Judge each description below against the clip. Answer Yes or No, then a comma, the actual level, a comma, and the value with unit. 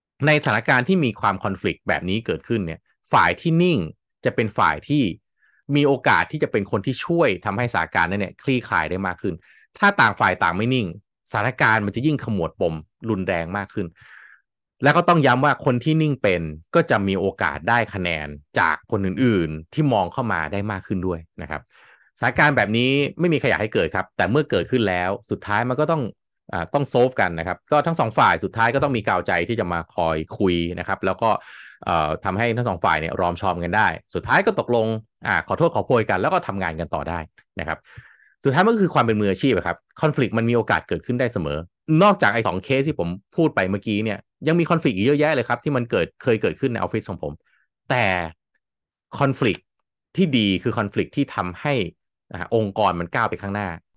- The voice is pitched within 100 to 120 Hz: Yes, low, 110 Hz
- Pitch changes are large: Yes, wide, 7.1 semitones